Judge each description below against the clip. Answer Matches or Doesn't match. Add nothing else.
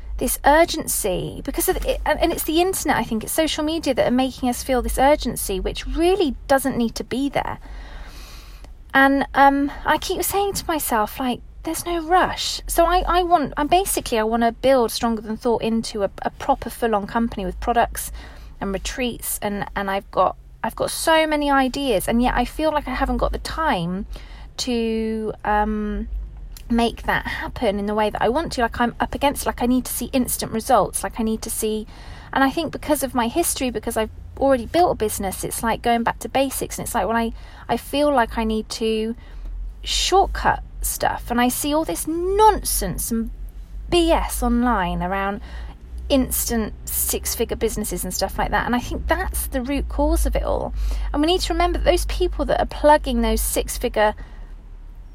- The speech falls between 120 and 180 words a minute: Doesn't match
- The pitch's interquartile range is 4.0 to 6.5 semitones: Matches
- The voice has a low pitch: Doesn't match